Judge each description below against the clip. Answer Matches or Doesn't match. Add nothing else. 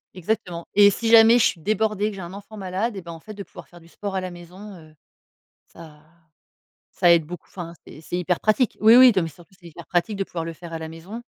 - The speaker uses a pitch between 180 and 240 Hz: Matches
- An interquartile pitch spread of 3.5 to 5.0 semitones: Matches